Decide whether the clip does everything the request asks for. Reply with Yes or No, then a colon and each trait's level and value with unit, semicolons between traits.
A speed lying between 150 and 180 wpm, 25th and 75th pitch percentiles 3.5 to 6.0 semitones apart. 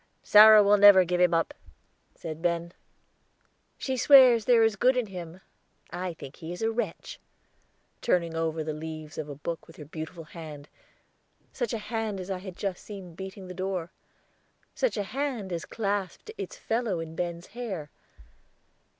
Yes: average, 165 wpm; average, 4.7 semitones